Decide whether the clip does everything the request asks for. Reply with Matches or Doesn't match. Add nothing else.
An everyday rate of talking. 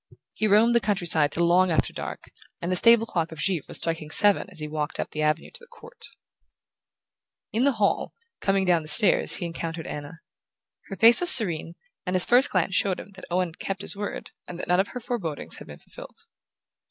Doesn't match